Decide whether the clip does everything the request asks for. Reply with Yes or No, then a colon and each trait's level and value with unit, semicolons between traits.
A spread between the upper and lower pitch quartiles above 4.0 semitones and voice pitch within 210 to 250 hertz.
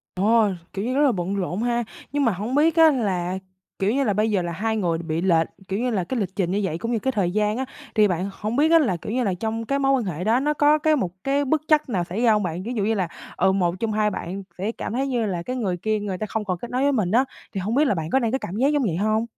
Yes: average, 5.2 semitones; high, 215 Hz